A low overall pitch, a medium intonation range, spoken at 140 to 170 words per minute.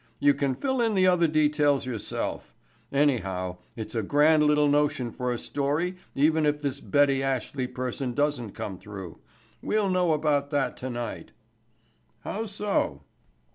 No: medium, 145 Hz; average, 3.5 semitones; average, 145 wpm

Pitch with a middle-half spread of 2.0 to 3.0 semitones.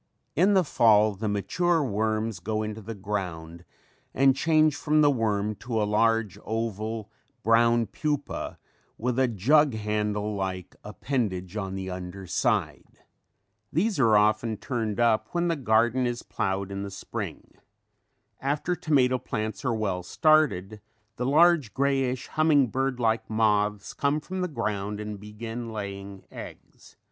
No: average, 4.5 semitones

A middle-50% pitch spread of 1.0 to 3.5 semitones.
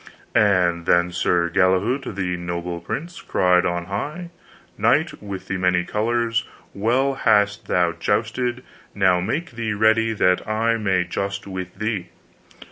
No: average, 4.1 semitones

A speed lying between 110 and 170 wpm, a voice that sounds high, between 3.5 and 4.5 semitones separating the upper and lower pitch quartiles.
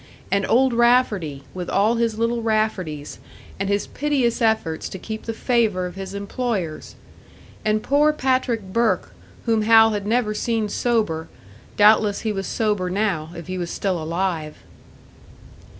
Yes: average, 150 wpm; high, 215 Hz; average, 3.9 semitones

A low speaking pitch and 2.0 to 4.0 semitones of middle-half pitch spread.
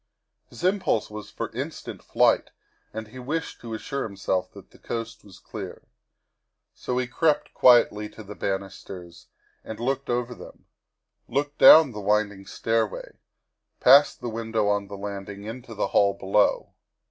Yes: low, 110 Hz; average, 3.6 semitones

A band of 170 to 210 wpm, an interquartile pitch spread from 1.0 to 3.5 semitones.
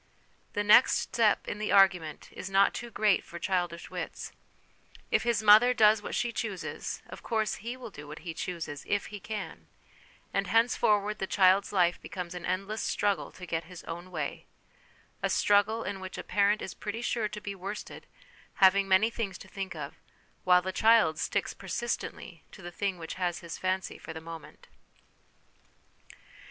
Yes: average, 175 wpm; average, 3.1 semitones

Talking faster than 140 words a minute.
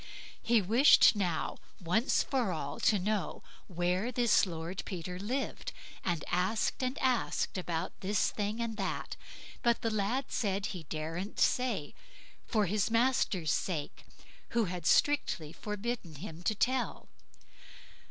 No: slow, 135 wpm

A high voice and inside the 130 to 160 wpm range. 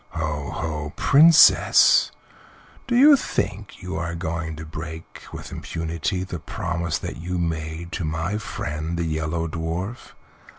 No: very low, 85 Hz; slow, 135 wpm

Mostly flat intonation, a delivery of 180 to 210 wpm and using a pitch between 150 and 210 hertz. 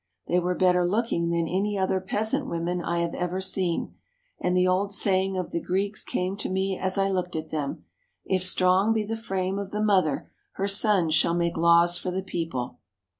Yes: narrow, 2.3 semitones; average, 200 wpm; medium, 185 Hz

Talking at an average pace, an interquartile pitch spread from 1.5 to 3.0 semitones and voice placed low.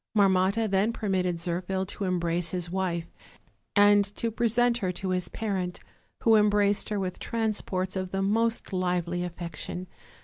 No: average, 145 wpm; average, 2.7 semitones; high, 190 Hz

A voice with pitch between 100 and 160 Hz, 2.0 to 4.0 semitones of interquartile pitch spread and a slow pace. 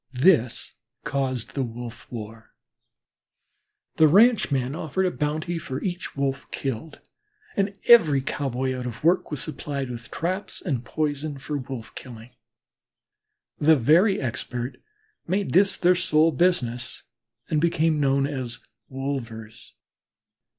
No: medium, 140 Hz; average, 4.6 semitones; slow, 120 wpm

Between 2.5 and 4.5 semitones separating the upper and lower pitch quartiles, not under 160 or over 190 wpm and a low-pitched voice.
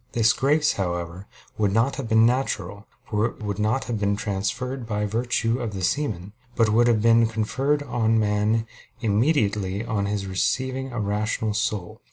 Yes: average, 2.9 semitones; average, 170 wpm; low, 110 Hz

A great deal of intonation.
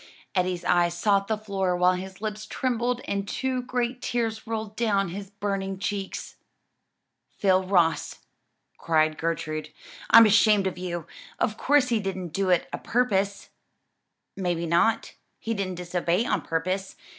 No: average, 3.5 semitones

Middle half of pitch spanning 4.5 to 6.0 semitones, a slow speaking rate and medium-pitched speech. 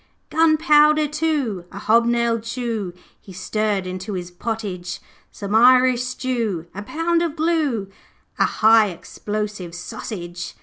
No: average, 5.2 semitones; slow, 125 wpm; high, 225 Hz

